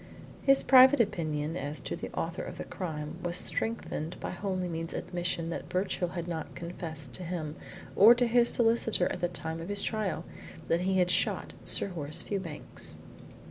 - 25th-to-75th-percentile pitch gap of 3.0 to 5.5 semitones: Yes, average, 3.4 semitones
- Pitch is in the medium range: Yes, medium, 175 Hz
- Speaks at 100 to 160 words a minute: No, average, 175 wpm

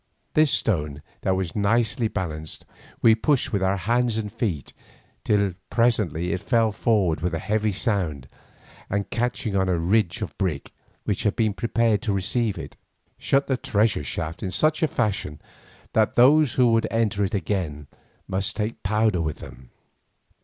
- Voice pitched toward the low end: Yes, low, 105 Hz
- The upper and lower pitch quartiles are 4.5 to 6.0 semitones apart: No, average, 4.0 semitones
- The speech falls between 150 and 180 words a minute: Yes, average, 165 wpm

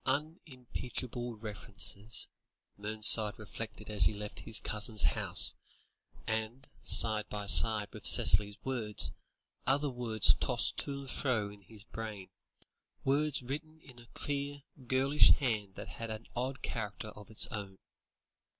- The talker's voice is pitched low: Yes, low, 110 Hz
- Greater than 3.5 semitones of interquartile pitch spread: Yes, average, 3.9 semitones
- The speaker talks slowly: Yes, slow, 130 wpm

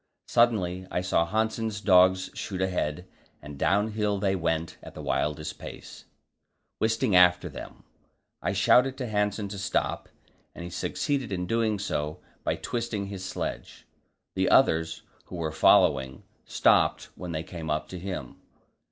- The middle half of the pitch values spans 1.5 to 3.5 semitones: No, average, 4.2 semitones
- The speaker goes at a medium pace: Yes, average, 145 wpm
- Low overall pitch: Yes, very low, 95 Hz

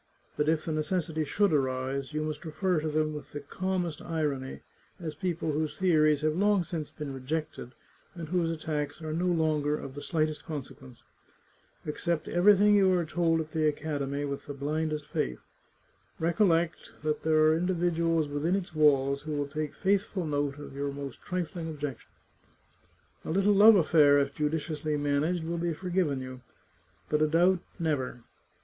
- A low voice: No, medium, 155 Hz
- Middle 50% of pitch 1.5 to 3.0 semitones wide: Yes, average, 2.7 semitones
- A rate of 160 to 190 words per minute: Yes, average, 170 wpm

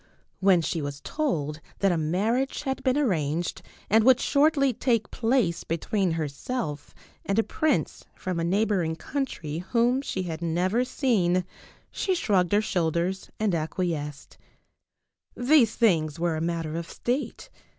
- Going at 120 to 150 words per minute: Yes, average, 140 wpm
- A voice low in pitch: No, medium, 185 Hz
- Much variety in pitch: Yes, wide, 6.7 semitones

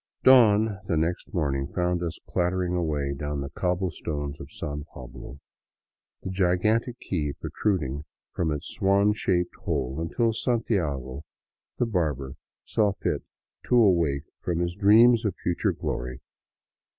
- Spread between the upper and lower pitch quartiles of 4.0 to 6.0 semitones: Yes, wide, 5.6 semitones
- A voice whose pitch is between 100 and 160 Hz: No, very low, 85 Hz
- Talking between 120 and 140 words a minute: Yes, slow, 135 wpm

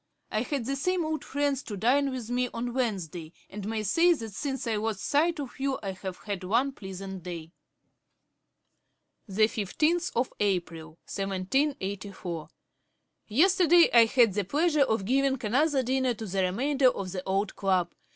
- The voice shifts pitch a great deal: Yes, wide, 6.1 semitones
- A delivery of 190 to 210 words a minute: No, average, 165 wpm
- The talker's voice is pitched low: No, high, 225 Hz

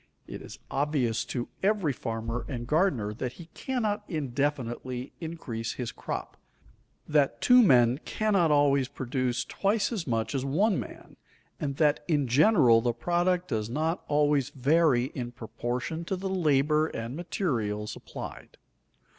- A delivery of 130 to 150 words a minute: Yes, average, 140 wpm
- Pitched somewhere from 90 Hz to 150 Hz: Yes, medium, 140 Hz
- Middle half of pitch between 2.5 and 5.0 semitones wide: No, wide, 5.6 semitones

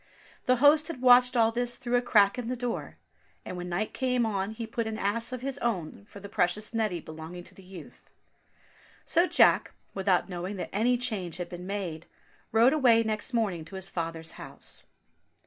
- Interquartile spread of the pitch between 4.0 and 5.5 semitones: Yes, average, 5.1 semitones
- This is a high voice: Yes, high, 215 Hz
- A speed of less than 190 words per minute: No, average, 195 wpm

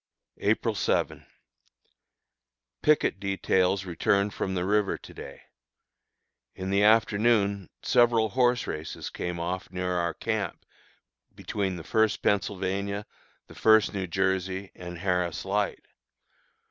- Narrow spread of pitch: Yes, narrow, 2.3 semitones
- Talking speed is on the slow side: Yes, slow, 115 wpm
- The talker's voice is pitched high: No, very low, 95 Hz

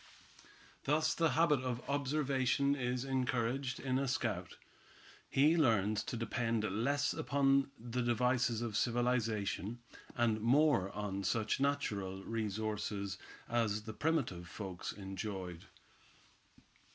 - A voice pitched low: Yes, low, 120 Hz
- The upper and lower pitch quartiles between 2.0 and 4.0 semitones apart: No, average, 4.5 semitones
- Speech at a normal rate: No, slow, 110 wpm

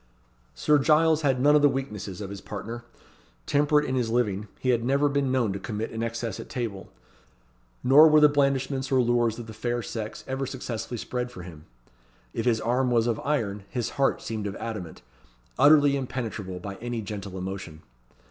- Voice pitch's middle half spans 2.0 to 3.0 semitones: No, average, 4.2 semitones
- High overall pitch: No, low, 120 Hz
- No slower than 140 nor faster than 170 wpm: No, average, 185 wpm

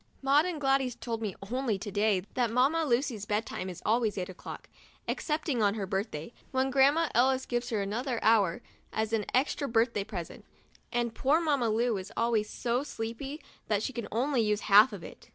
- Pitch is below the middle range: No, high, 235 Hz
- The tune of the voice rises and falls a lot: No, average, 4.1 semitones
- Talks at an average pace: Yes, average, 190 wpm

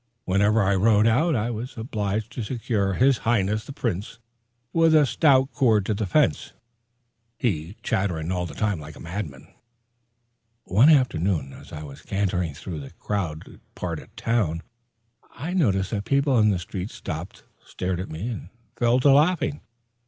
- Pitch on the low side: Yes, low, 105 Hz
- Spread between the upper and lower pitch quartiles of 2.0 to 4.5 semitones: No, average, 5.2 semitones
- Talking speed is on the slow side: No, average, 170 wpm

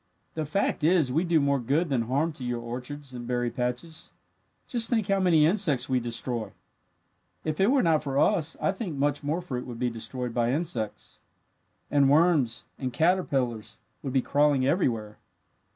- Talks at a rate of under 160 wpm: No, average, 175 wpm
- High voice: No, medium, 140 Hz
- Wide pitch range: No, average, 5.0 semitones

